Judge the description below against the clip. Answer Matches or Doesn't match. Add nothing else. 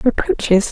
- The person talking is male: Doesn't match